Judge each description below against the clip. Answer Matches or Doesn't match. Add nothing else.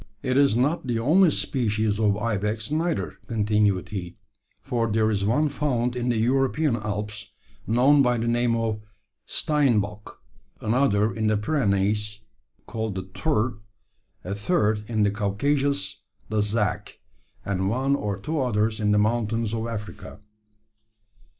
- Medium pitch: Doesn't match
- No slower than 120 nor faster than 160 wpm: Matches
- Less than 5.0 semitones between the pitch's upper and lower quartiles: Matches